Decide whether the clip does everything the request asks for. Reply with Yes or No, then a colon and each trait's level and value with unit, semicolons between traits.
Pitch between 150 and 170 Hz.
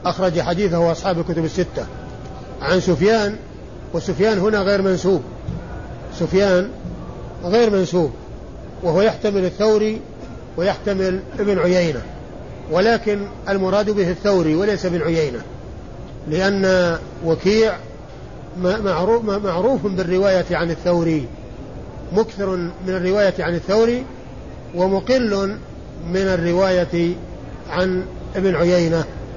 No: medium, 185 Hz